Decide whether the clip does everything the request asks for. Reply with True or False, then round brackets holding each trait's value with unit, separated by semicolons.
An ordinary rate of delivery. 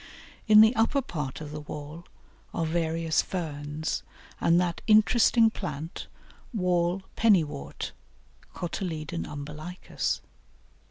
False (100 wpm)